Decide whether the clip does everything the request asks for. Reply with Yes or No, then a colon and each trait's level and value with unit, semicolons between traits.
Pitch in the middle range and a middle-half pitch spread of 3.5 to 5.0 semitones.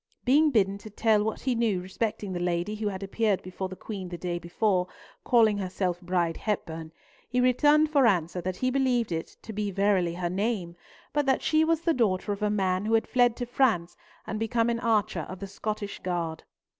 No: high, 205 Hz; average, 4.2 semitones